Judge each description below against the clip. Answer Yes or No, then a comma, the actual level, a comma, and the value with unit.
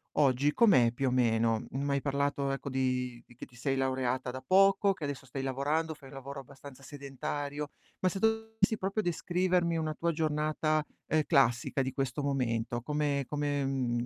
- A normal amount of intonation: Yes, average, 3.1 semitones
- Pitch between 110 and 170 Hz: Yes, medium, 140 Hz